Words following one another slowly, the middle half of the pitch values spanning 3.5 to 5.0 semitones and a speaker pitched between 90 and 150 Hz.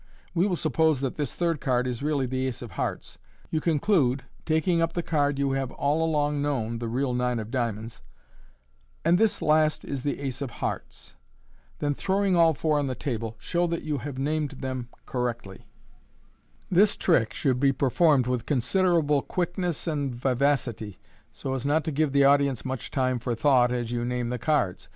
No: average, 190 wpm; average, 4.0 semitones; medium, 140 Hz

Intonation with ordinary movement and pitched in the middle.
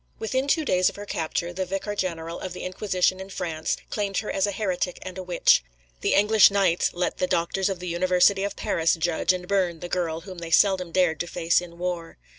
No: narrow, 2.2 semitones; medium, 180 Hz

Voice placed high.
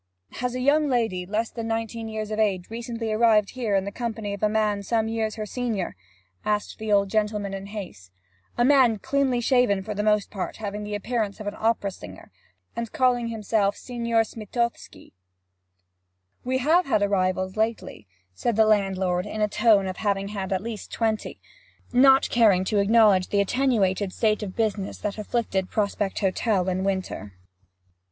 Yes: high, 215 Hz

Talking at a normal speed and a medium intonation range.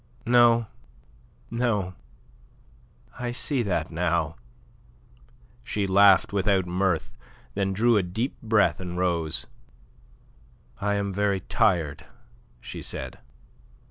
No: slow, 100 wpm; average, 3.8 semitones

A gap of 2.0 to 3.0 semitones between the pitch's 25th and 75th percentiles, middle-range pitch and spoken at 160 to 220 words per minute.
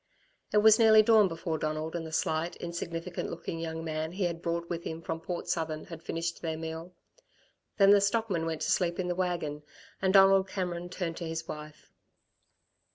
Yes: narrow, 2.4 semitones; medium, 170 Hz; average, 190 wpm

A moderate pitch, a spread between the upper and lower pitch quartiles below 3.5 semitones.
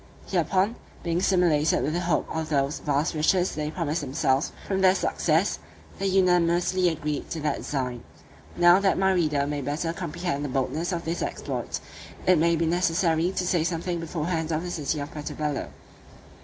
Yes: medium, 165 Hz; average, 2.9 semitones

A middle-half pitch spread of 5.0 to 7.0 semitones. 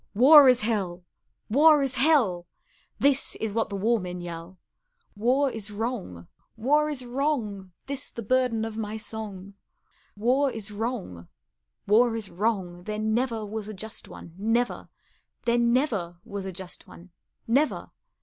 No: average, 4.3 semitones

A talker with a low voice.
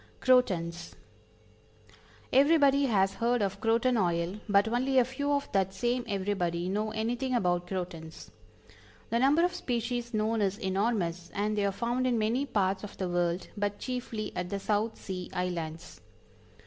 No: high, 210 Hz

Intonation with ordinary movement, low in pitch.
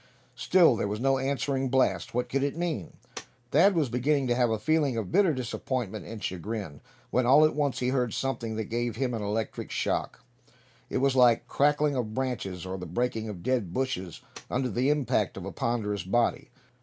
Yes: average, 3.8 semitones; low, 125 Hz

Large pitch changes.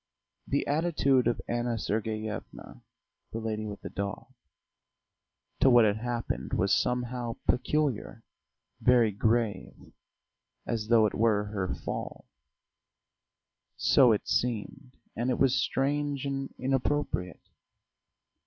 No: average, 3.4 semitones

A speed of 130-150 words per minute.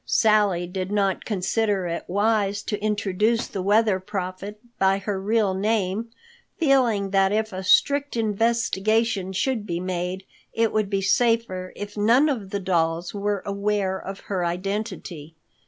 Yes: average, 145 wpm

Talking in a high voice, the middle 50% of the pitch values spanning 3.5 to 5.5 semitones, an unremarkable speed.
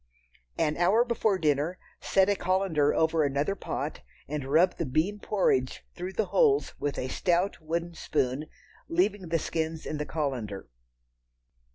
No: medium, 165 Hz; average, 4.3 semitones; average, 150 wpm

